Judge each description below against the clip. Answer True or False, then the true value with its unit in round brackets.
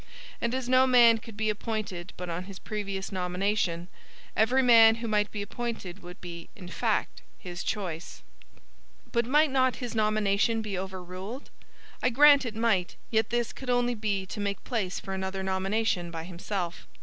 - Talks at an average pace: True (170 wpm)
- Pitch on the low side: False (210 Hz)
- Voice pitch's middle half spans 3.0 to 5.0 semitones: True (3.9 semitones)